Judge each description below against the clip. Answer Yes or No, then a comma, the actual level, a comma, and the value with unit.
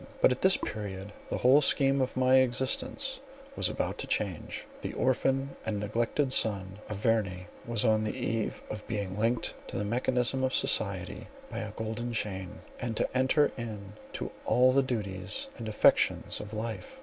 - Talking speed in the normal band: Yes, average, 170 wpm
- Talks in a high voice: No, low, 115 Hz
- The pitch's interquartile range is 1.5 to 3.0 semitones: No, average, 3.7 semitones